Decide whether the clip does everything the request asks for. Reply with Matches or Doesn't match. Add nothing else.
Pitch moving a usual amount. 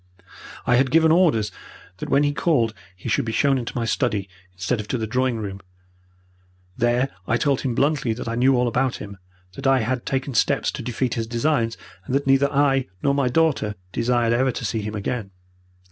Matches